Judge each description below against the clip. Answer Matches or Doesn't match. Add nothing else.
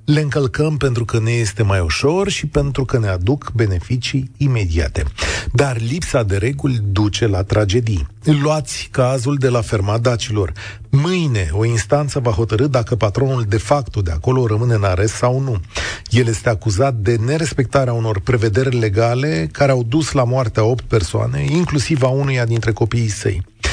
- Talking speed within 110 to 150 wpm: Doesn't match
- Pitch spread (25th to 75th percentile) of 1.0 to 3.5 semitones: Doesn't match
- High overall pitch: Doesn't match